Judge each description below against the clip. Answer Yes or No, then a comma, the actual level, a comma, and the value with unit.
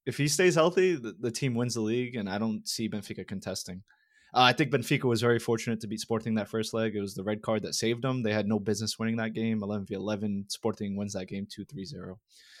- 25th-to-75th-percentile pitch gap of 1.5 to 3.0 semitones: Yes, narrow, 2.4 semitones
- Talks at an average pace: No, fast, 250 wpm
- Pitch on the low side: Yes, low, 110 Hz